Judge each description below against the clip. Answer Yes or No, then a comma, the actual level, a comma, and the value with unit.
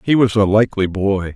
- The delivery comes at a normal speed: No, fast, 220 wpm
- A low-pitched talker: Yes, low, 100 Hz